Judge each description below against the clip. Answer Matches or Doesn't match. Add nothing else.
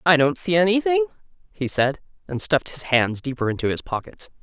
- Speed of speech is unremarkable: Matches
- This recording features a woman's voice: Matches